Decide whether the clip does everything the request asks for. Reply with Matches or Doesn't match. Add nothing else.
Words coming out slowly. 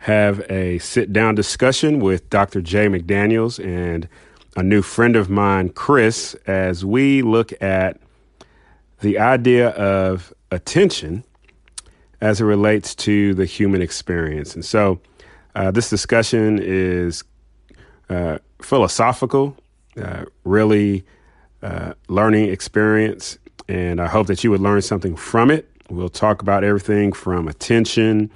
Matches